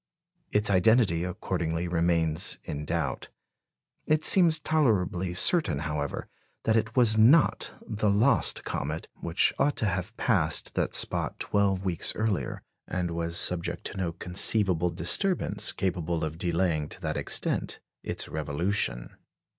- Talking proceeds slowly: Yes, slow, 130 wpm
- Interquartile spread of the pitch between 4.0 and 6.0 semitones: Yes, average, 4.6 semitones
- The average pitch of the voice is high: No, very low, 90 Hz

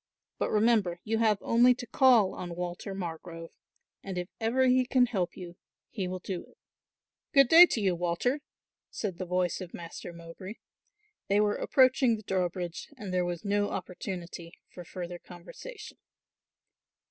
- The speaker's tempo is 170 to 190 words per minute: No, average, 160 wpm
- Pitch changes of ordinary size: Yes, average, 4.6 semitones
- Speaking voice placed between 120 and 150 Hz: No, high, 190 Hz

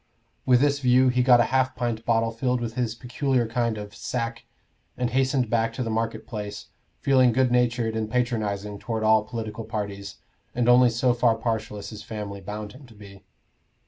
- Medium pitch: No, low, 115 Hz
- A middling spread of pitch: No, narrow, 2.3 semitones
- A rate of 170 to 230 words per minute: Yes, average, 190 wpm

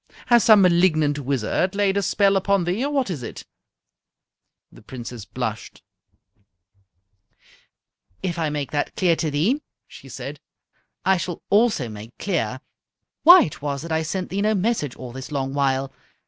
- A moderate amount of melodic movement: No, wide, 6.3 semitones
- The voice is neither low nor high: Yes, medium, 165 Hz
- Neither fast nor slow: Yes, average, 160 wpm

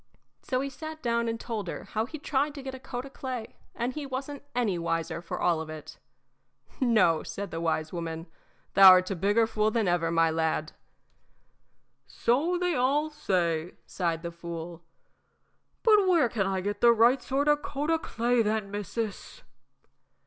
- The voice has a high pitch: Yes, high, 220 Hz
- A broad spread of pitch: Yes, wide, 7.6 semitones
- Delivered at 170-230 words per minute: Yes, average, 180 wpm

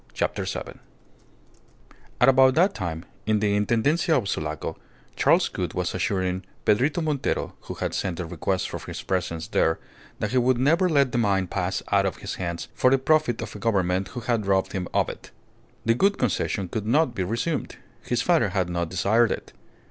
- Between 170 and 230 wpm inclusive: Yes, average, 190 wpm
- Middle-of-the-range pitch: No, low, 105 Hz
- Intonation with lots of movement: Yes, wide, 5.7 semitones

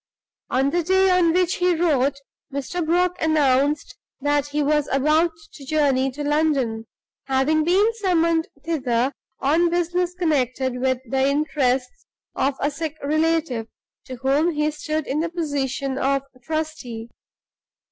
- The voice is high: Yes, very high, 295 Hz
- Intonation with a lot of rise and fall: No, average, 3.6 semitones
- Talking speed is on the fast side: No, slow, 135 wpm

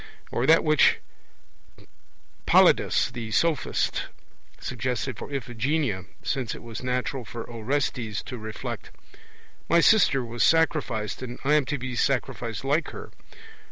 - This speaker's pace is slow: Yes, slow, 125 wpm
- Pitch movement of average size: Yes, average, 3.7 semitones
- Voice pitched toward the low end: Yes, low, 125 Hz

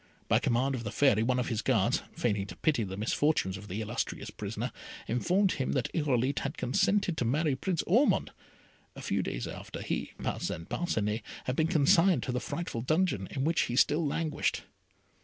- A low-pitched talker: Yes, low, 130 Hz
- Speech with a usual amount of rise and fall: No, wide, 5.8 semitones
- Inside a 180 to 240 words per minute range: Yes, average, 185 wpm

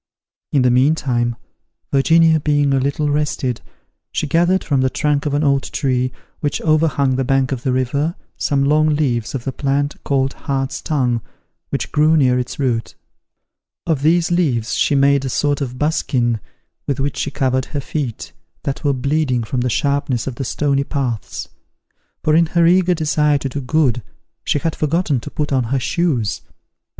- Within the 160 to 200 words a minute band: Yes, average, 175 wpm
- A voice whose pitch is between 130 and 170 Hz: Yes, medium, 140 Hz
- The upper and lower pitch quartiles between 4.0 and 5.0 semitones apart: No, average, 2.8 semitones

